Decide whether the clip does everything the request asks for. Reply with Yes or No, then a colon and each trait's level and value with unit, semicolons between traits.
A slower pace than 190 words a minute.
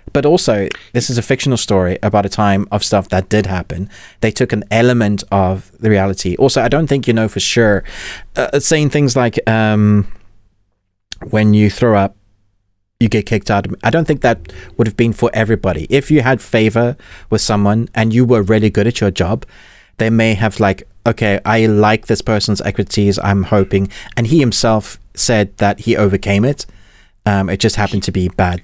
No: average, 195 wpm